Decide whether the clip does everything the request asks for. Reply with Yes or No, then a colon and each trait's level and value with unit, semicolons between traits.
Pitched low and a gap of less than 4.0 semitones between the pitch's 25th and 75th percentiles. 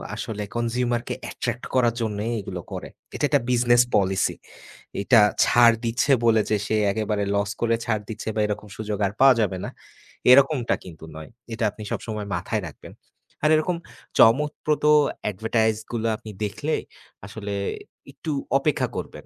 Yes: low, 115 Hz; average, 2.8 semitones